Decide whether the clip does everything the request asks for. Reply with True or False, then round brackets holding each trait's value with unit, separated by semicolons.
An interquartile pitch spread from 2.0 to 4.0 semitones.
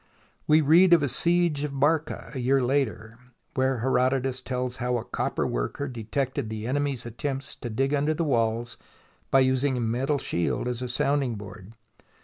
True (3.2 semitones)